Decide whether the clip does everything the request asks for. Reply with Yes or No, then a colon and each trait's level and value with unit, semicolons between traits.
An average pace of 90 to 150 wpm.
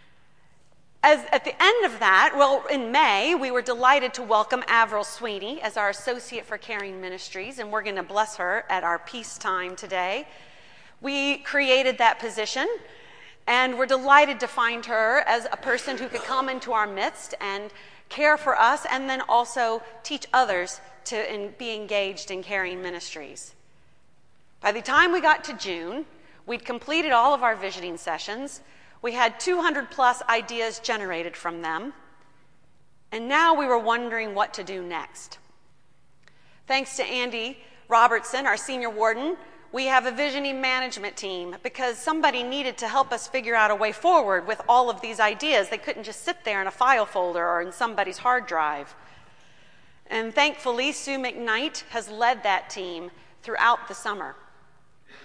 No: average, 165 wpm